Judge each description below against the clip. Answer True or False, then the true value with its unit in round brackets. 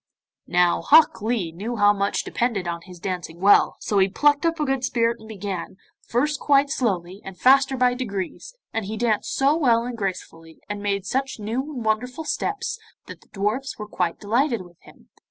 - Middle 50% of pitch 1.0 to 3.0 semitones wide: False (5.3 semitones)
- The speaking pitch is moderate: False (220 Hz)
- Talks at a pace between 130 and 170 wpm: False (190 wpm)